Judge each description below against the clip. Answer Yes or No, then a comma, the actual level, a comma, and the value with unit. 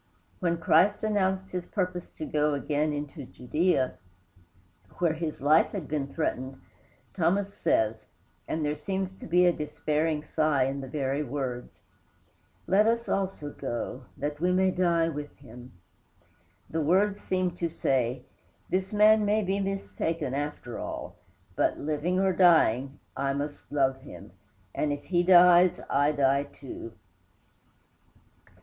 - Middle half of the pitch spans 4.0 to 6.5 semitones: Yes, average, 4.6 semitones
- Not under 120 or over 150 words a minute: Yes, average, 140 wpm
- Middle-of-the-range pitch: Yes, medium, 155 Hz